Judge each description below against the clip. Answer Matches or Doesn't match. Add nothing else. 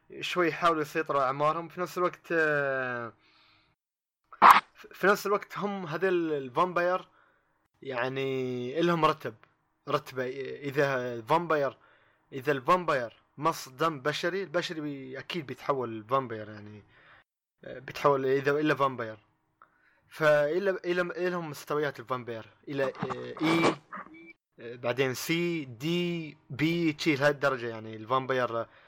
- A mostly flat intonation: Doesn't match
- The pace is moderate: Matches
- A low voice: Doesn't match